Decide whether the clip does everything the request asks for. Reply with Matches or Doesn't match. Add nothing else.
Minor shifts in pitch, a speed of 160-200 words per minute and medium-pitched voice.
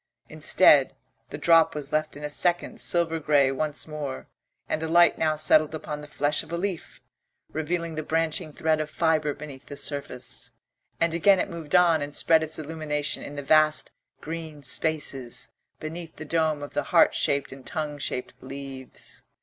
Matches